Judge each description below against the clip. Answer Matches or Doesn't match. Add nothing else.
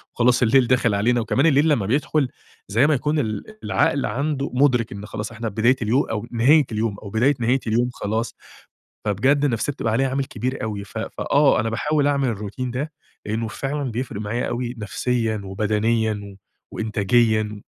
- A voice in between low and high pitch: Doesn't match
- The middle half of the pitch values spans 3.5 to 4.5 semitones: Matches